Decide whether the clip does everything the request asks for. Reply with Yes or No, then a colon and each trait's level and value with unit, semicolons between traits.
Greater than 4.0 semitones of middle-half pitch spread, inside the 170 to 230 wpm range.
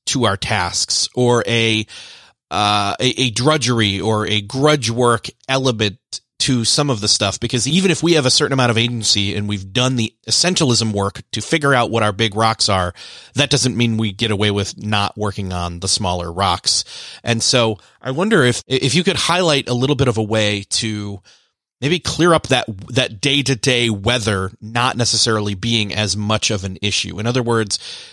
No: average, 3.7 semitones; average, 195 wpm